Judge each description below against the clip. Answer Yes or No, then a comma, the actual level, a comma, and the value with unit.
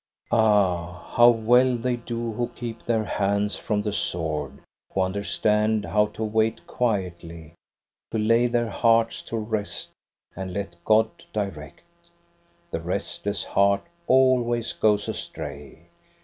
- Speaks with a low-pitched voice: Yes, low, 105 Hz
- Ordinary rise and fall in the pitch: Yes, average, 3.0 semitones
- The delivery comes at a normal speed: No, slow, 125 wpm